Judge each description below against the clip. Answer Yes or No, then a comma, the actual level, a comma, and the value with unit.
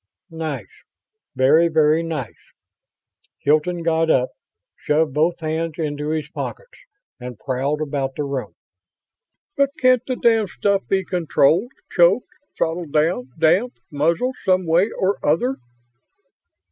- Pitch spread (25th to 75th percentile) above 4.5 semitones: No, average, 3.8 semitones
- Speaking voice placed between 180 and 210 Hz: No, medium, 160 Hz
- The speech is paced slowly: Yes, slow, 120 wpm